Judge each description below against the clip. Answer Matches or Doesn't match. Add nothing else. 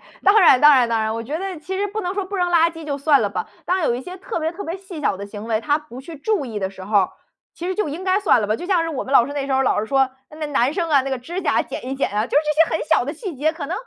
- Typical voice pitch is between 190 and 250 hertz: Doesn't match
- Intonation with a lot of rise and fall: Matches